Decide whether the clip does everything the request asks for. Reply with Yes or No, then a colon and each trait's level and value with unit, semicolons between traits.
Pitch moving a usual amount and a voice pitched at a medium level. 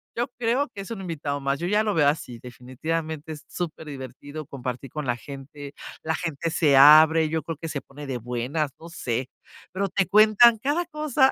No: wide, 5.7 semitones; medium, 155 Hz